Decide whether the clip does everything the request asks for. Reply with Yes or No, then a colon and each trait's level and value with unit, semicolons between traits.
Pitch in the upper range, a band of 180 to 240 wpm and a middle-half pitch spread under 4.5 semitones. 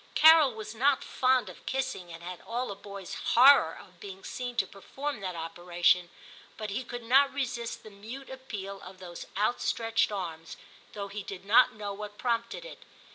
No: high, 210 Hz; average, 185 wpm; average, 4.8 semitones